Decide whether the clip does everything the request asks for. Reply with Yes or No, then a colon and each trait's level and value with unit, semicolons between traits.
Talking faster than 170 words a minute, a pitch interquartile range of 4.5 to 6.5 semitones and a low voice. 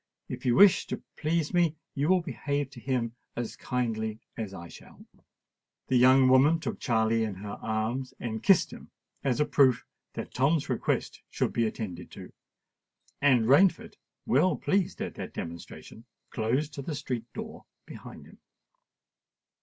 No: average, 155 wpm; average, 4.9 semitones; low, 130 Hz